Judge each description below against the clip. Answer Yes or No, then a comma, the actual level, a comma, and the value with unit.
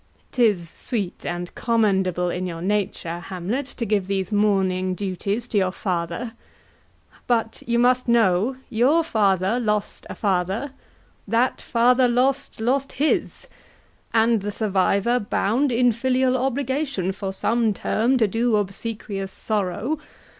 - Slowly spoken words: Yes, slow, 130 wpm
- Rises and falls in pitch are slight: No, average, 4.2 semitones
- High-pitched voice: Yes, high, 215 Hz